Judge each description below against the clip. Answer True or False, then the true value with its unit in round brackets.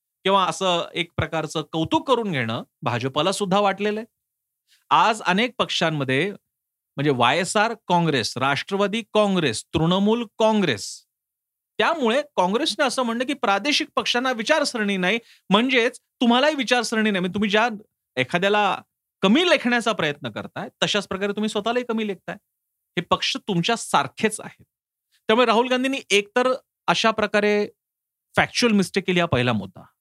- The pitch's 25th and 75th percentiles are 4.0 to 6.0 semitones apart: True (5.1 semitones)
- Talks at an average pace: False (135 wpm)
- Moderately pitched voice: False (205 Hz)